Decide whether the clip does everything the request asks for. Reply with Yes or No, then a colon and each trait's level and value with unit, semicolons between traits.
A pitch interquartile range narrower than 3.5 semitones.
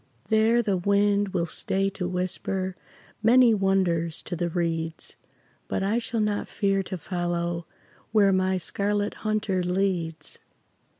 Yes: average, 2.8 semitones